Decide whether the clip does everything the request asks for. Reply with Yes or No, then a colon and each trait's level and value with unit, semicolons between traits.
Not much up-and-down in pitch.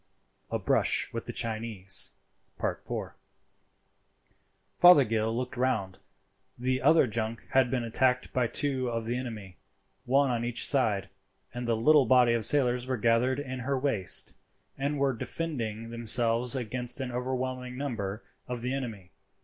Yes: narrow, 2.2 semitones